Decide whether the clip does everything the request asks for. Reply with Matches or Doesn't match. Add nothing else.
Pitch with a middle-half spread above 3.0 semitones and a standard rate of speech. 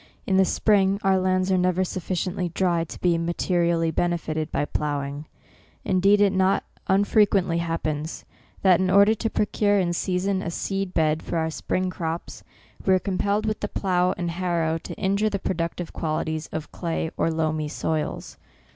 Doesn't match